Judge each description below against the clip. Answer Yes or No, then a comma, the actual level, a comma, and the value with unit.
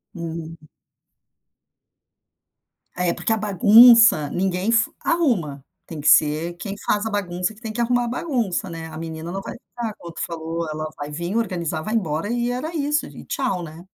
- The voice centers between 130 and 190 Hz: Yes, medium, 185 Hz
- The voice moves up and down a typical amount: No, wide, 5.8 semitones